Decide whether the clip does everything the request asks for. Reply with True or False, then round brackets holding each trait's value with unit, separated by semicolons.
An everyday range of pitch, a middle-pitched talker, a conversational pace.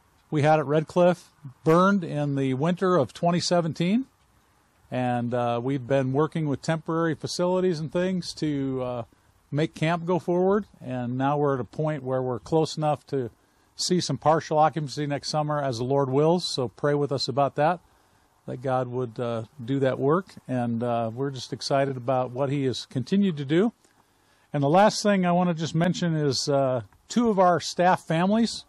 True (4.9 semitones; 145 Hz; 185 wpm)